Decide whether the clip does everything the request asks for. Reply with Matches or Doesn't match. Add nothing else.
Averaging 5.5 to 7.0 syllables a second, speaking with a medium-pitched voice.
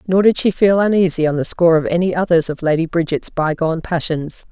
Matches